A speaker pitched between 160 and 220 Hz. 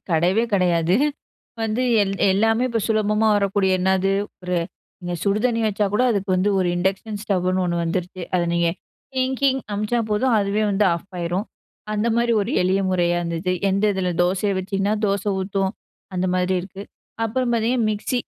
Yes: high, 195 Hz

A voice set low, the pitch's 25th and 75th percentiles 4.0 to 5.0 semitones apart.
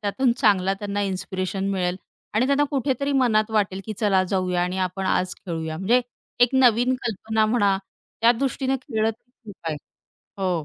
No: high, 210 Hz; average, 4.6 semitones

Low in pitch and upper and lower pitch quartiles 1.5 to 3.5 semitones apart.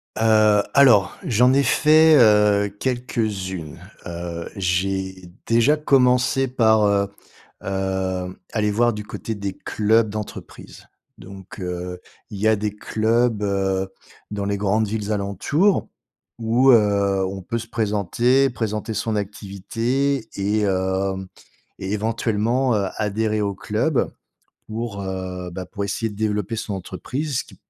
Yes: low, 105 Hz; average, 3.0 semitones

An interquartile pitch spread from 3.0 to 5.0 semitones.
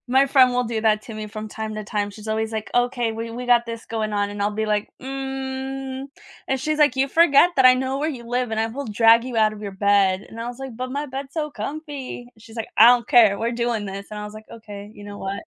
Yes: average, 3.6 semitones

